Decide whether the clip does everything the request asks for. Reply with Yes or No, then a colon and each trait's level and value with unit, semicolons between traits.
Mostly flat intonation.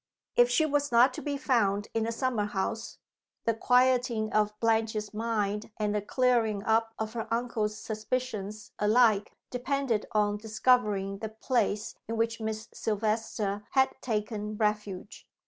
Yes: narrow, 2.3 semitones